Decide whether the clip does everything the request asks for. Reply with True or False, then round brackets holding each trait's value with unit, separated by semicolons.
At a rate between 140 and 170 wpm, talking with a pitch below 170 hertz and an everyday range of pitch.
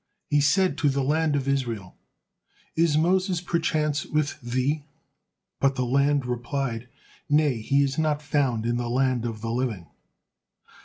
True (150 wpm; 140 Hz; 3.8 semitones)